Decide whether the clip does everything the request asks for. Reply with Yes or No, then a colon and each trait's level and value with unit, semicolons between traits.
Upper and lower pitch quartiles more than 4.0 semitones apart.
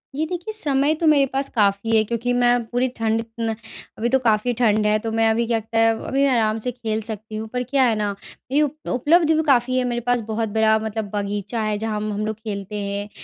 No: average, 2.8 semitones